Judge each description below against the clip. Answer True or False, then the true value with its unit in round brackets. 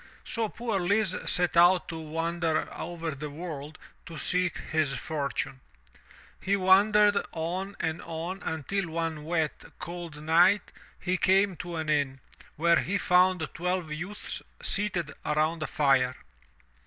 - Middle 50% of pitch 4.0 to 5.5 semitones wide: False (3.0 semitones)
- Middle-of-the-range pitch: True (170 Hz)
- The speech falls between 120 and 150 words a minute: True (135 wpm)